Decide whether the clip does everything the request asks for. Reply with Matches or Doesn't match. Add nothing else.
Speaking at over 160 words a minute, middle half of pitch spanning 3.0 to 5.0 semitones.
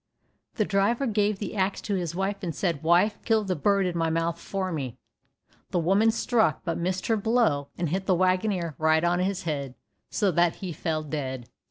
Matches